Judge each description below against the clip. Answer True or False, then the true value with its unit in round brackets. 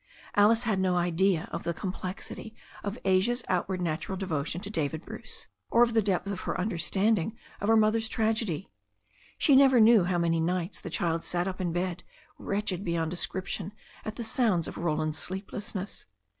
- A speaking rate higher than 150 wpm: True (170 wpm)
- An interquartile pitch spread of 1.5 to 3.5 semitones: False (3.9 semitones)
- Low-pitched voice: False (190 Hz)